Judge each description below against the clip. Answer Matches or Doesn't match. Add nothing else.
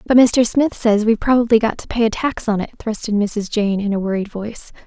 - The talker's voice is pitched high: Matches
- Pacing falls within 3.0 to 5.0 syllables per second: Doesn't match